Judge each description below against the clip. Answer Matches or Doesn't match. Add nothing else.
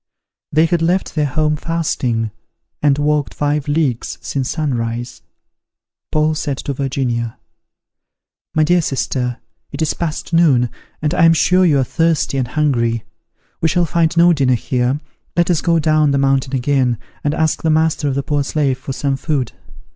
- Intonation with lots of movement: Doesn't match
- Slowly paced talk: Doesn't match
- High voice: Doesn't match